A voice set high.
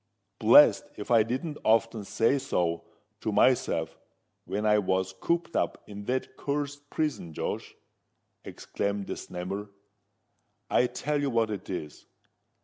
No: low, 110 Hz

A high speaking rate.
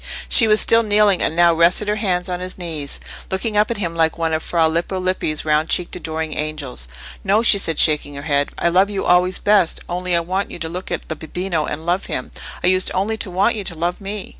Yes: fast, 240 wpm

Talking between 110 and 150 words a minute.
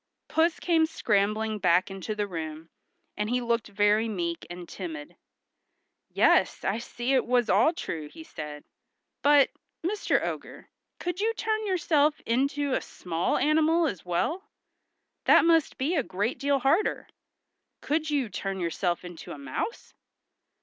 Yes: average, 145 wpm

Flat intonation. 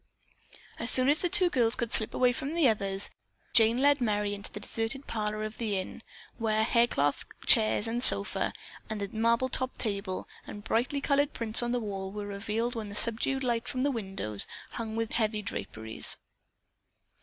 No: average, 3.1 semitones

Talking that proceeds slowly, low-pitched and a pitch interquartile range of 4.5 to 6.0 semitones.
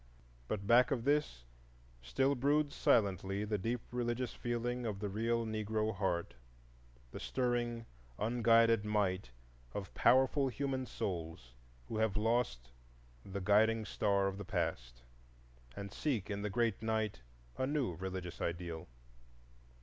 No: slow, 130 wpm; low, 110 Hz; average, 3.6 semitones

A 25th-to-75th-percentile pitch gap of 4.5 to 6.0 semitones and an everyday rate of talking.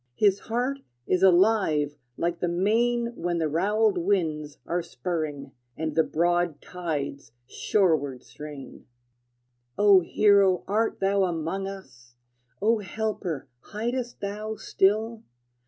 No: average, 4.8 semitones; slow, 115 wpm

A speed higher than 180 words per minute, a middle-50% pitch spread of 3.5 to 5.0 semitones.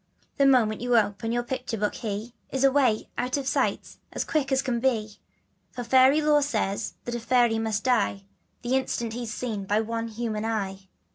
No: average, 190 wpm; average, 3.1 semitones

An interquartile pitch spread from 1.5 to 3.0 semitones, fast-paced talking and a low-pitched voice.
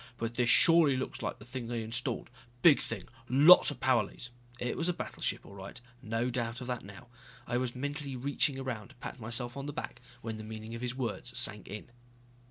Yes: narrow, 2.6 semitones; fast, 220 wpm; low, 120 Hz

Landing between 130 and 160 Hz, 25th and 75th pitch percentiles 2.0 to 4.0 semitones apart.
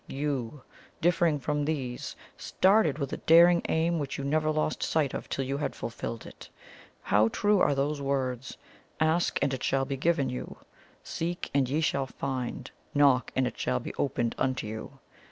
Yes: medium, 140 Hz; average, 3.3 semitones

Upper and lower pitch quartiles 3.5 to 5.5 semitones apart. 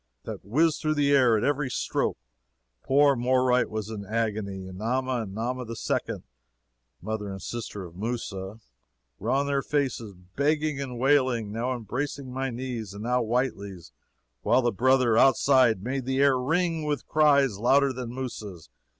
Yes: average, 4.0 semitones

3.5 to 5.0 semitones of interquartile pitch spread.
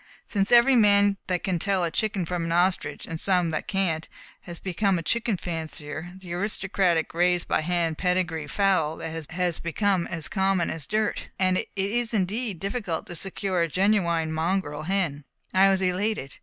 No: average, 3.1 semitones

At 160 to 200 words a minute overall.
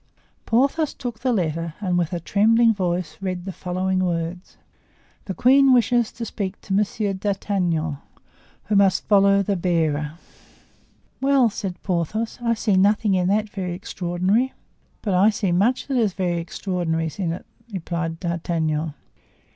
No: average, 145 wpm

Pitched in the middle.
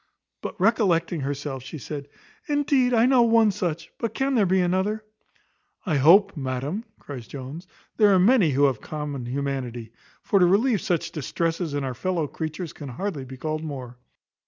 Yes: medium, 165 Hz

